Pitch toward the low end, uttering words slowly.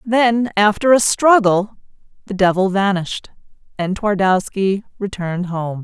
No: high, 200 Hz; slow, 115 wpm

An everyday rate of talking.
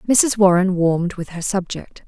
Yes: average, 175 wpm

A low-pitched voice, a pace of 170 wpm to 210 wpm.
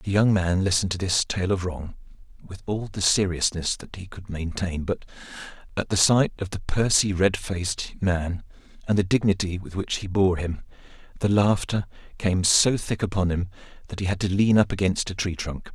Yes: very low, 95 Hz; average, 200 wpm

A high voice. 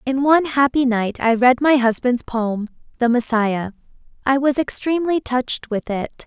Yes: very high, 250 Hz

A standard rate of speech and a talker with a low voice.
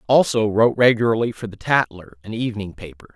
Yes: average, 170 wpm; low, 110 Hz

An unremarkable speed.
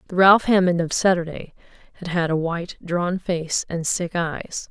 Yes: average, 180 wpm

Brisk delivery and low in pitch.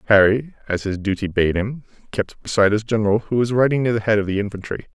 Yes: fast, 230 wpm; low, 110 Hz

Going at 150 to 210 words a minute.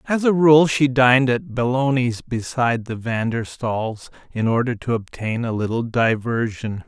Yes: average, 165 wpm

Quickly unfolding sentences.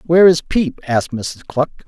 No: average, 190 wpm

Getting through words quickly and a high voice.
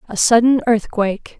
No: slow, 130 wpm; high, 225 Hz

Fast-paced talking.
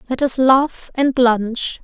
No: average, 165 wpm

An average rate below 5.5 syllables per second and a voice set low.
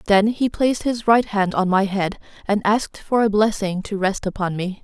No: 5.1 syllables/s; high, 205 Hz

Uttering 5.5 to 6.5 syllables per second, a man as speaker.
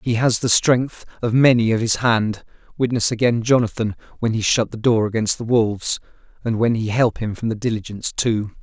No: 5.2 syllables/s; male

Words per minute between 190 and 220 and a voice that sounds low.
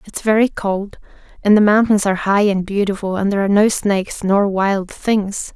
No: average, 195 wpm; high, 200 Hz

